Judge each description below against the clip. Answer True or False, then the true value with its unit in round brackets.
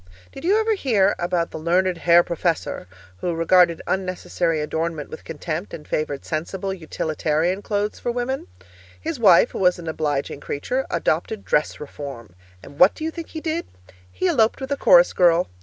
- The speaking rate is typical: True (175 wpm)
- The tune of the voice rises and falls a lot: True (6.3 semitones)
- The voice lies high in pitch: False (175 Hz)